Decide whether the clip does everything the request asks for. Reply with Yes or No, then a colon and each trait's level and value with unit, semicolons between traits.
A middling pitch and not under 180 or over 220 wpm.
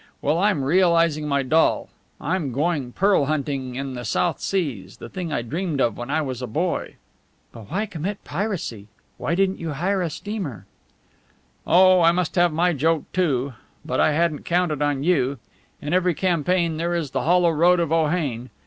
Yes: medium, 160 Hz; average, 185 wpm